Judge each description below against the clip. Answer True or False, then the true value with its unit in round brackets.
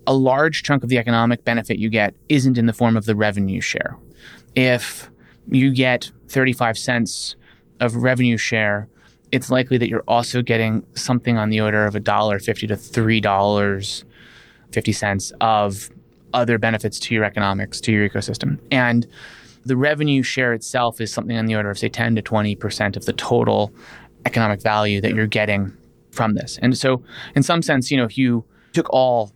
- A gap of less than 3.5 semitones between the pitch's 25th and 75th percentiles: True (2.8 semitones)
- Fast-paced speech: False (175 wpm)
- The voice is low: True (115 Hz)